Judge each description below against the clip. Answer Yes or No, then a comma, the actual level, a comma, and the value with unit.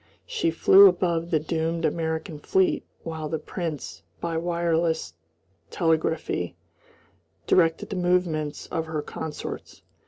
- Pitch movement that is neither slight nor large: No, narrow, 1.4 semitones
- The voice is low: No, medium, 165 Hz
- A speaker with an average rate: No, slow, 115 wpm